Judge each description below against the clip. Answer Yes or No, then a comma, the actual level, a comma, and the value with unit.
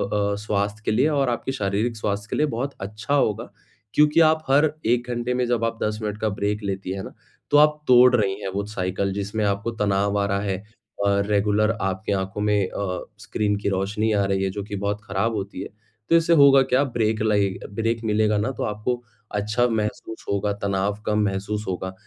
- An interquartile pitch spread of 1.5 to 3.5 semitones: Yes, average, 2.9 semitones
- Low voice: Yes, low, 105 Hz